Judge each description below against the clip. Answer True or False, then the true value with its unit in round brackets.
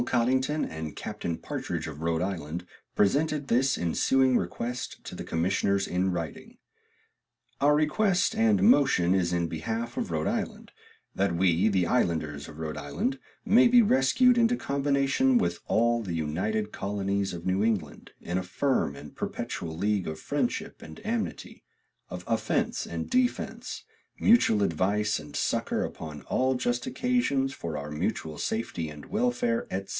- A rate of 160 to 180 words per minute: False (150 wpm)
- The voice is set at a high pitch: False (100 Hz)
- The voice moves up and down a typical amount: False (8.3 semitones)